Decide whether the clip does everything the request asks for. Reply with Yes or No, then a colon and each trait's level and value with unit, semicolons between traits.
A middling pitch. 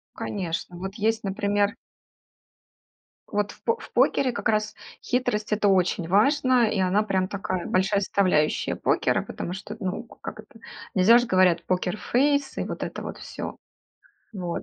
No: high, 200 Hz